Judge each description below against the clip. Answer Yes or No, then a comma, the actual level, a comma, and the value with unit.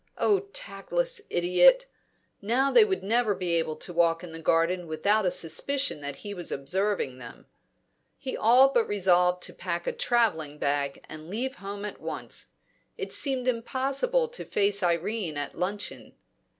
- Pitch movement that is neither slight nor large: No, wide, 7.4 semitones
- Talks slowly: No, average, 160 wpm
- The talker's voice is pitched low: No, high, 200 Hz